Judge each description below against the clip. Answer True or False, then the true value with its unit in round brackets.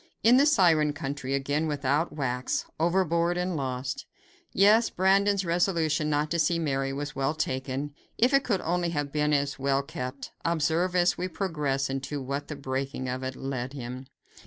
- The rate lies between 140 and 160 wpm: False (170 wpm)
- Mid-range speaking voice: True (150 Hz)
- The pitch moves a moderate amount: True (4.2 semitones)